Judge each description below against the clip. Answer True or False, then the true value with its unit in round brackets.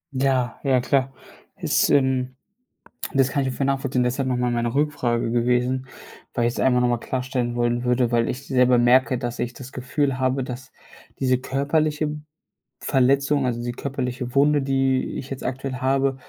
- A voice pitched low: True (130 Hz)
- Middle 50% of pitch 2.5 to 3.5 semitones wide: False (1.8 semitones)